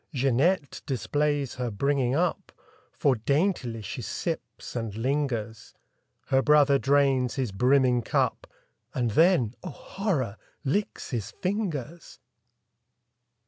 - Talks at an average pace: No, slow, 100 wpm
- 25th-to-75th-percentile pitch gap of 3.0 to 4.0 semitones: Yes, average, 3.6 semitones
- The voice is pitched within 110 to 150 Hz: Yes, low, 135 Hz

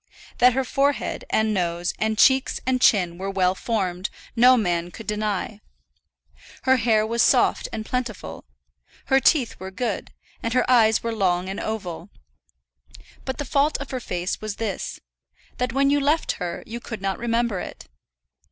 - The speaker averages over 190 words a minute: No, average, 165 wpm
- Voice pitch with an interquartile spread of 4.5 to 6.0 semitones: Yes, average, 4.8 semitones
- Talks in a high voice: Yes, high, 220 Hz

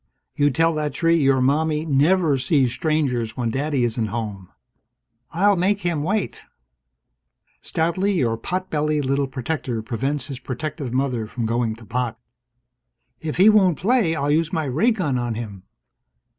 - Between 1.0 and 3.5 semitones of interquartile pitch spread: No, average, 5.1 semitones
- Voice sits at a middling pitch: Yes, medium, 145 Hz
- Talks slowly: No, average, 155 wpm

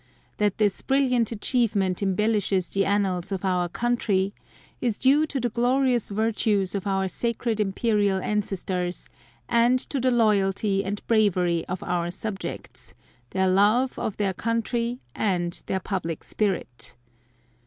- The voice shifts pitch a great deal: No, average, 3.5 semitones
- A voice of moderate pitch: No, high, 205 Hz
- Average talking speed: No, slow, 130 wpm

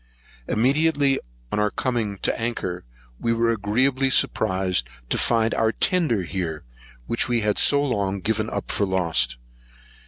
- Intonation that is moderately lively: Yes, average, 4.8 semitones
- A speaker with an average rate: Yes, average, 145 wpm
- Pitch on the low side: Yes, low, 110 Hz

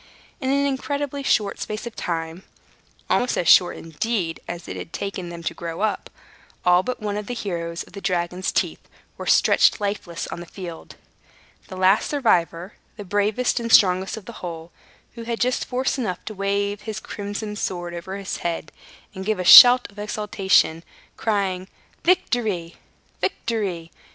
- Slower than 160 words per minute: No, average, 165 wpm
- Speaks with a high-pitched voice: Yes, high, 200 Hz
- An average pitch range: Yes, average, 4.2 semitones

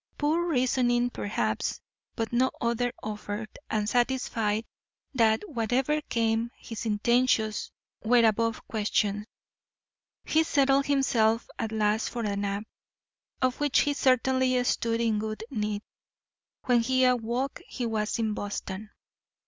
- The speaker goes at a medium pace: No, slow, 125 wpm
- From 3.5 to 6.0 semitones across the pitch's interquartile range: No, average, 3.0 semitones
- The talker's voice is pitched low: No, high, 230 Hz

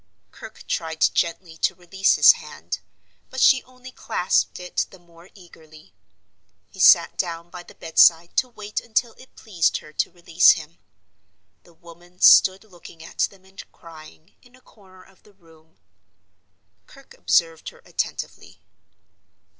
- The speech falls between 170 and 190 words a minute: No, average, 145 wpm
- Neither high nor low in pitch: Yes, medium, 175 Hz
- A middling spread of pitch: Yes, average, 3.1 semitones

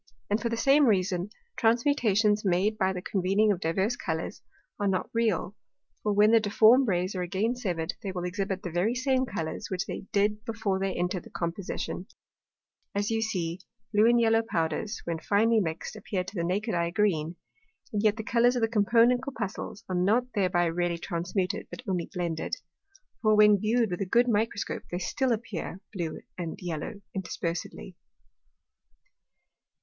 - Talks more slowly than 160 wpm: No, average, 170 wpm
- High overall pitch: Yes, high, 200 Hz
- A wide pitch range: No, average, 3.9 semitones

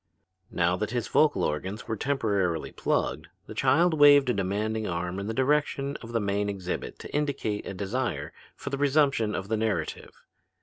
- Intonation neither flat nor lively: No, wide, 5.8 semitones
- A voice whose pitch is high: No, low, 110 Hz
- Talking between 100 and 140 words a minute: No, average, 175 wpm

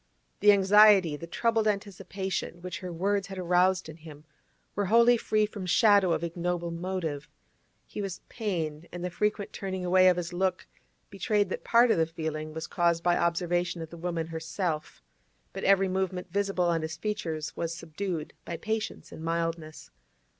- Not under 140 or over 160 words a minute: No, average, 170 wpm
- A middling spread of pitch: Yes, average, 3.0 semitones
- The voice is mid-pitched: Yes, medium, 180 Hz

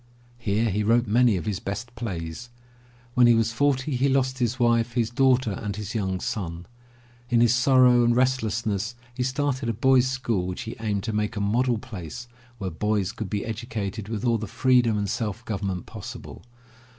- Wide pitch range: No, average, 3.2 semitones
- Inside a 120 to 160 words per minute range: No, average, 185 wpm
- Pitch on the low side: Yes, low, 115 Hz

